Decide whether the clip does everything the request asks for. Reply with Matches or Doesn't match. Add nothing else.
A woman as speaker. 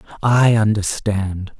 Doesn't match